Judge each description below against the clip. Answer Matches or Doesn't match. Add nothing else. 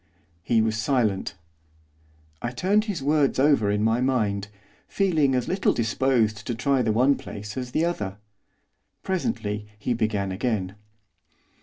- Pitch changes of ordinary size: Matches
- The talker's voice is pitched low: Matches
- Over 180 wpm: Doesn't match